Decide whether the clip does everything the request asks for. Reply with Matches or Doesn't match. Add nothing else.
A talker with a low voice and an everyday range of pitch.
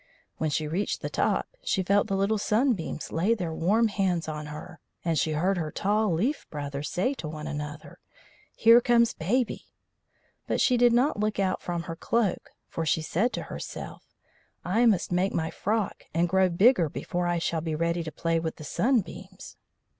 Doesn't match